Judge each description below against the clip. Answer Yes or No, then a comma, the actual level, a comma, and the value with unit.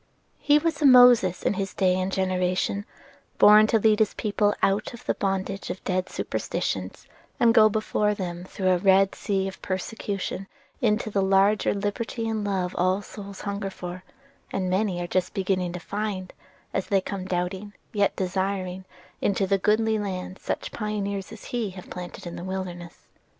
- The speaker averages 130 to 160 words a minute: No, average, 170 wpm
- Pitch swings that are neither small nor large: No, narrow, 2.2 semitones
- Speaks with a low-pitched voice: No, high, 195 Hz